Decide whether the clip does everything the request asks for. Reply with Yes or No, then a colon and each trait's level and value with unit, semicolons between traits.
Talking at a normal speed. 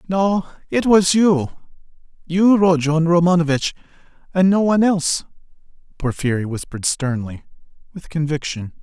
No: slow, 110 wpm